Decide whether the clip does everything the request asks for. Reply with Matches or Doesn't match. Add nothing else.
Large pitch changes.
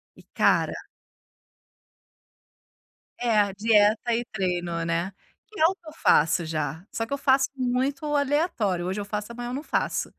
Matches